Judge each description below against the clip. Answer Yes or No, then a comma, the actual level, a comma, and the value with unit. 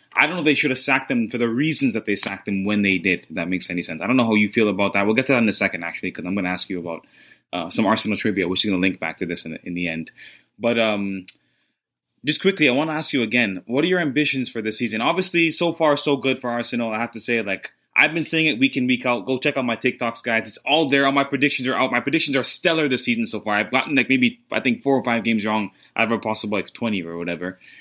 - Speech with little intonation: No, wide, 5.6 semitones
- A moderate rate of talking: No, fast, 305 wpm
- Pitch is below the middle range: Yes, low, 115 Hz